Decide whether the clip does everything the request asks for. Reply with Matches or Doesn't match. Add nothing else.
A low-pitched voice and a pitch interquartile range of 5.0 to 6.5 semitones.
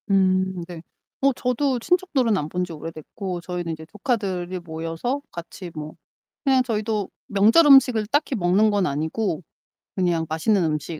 Doesn't match